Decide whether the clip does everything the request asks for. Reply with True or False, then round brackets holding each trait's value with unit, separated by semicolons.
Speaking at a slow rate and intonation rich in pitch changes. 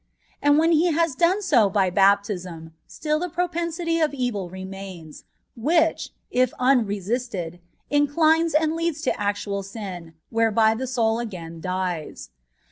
True (130 wpm; 8.5 semitones)